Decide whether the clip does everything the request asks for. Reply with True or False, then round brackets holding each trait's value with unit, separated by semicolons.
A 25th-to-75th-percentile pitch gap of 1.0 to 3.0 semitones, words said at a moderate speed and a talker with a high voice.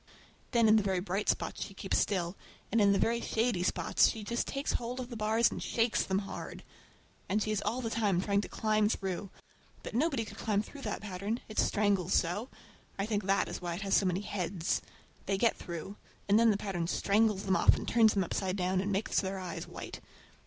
False (2.7 semitones; 220 wpm; 205 Hz)